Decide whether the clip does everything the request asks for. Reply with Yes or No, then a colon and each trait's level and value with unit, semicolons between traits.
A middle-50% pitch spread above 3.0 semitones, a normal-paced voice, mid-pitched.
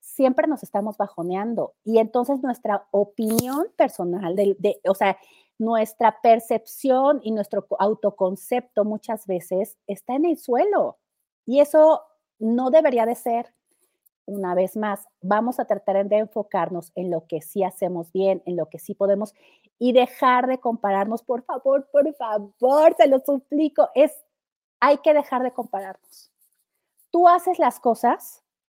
No: average, 5.3 semitones; average, 145 wpm; high, 225 Hz